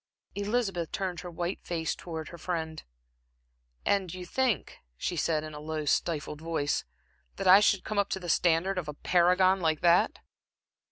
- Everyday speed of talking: Yes, average, 170 wpm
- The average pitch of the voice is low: No, medium, 175 Hz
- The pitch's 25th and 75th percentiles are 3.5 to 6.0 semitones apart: No, average, 2.9 semitones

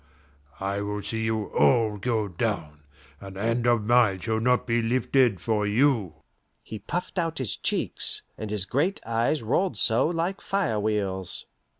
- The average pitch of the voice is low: Yes, low, 110 Hz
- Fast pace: No, average, 160 wpm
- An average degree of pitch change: Yes, average, 3.5 semitones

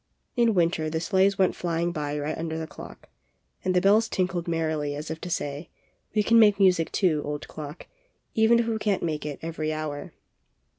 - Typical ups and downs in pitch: Yes, average, 3.9 semitones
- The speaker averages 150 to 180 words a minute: No, average, 195 wpm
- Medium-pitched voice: Yes, medium, 165 Hz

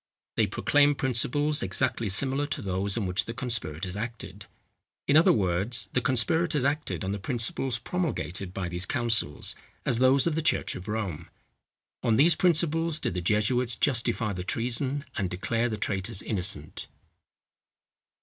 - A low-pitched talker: Yes, low, 115 Hz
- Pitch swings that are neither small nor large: No, wide, 6.4 semitones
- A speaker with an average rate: Yes, average, 150 wpm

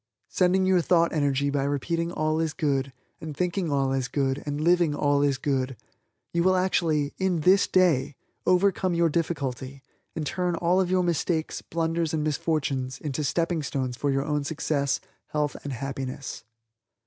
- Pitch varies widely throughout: No, average, 3.7 semitones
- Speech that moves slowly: No, average, 165 wpm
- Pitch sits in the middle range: Yes, medium, 155 Hz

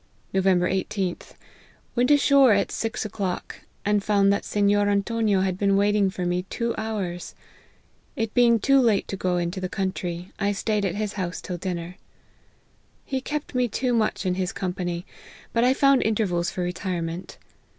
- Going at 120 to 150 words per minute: No, average, 170 wpm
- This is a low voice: No, high, 200 Hz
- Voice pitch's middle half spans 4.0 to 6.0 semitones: No, average, 3.4 semitones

